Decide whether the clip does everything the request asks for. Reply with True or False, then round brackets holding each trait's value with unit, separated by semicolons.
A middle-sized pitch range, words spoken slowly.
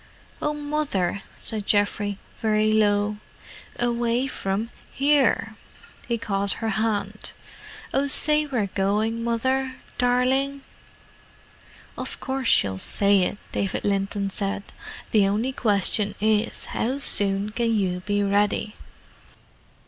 True (3.7 semitones; 105 wpm)